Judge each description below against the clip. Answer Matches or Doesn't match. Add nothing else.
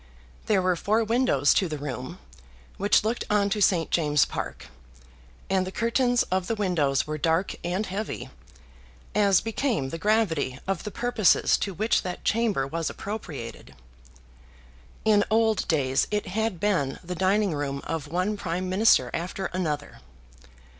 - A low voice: Doesn't match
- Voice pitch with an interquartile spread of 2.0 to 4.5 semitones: Doesn't match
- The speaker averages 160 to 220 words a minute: Doesn't match